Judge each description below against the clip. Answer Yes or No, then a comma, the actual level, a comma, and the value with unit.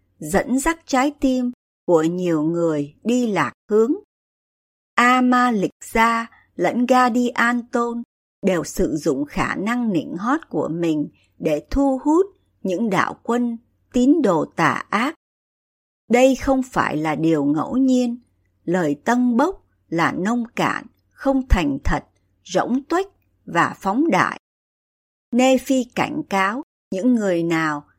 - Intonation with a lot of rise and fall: Yes, wide, 6.8 semitones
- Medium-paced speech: No, slow, 135 wpm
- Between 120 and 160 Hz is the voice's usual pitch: No, high, 240 Hz